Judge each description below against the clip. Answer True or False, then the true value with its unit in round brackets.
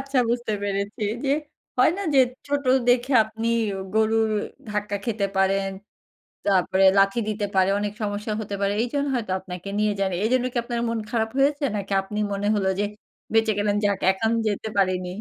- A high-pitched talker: True (210 Hz)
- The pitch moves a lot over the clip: False (2.9 semitones)